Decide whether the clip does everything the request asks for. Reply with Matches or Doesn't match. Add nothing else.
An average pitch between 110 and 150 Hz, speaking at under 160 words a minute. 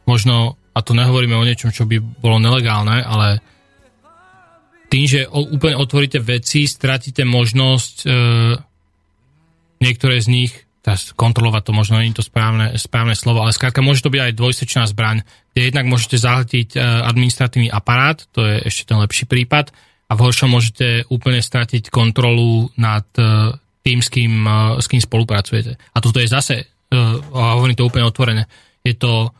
Doesn't match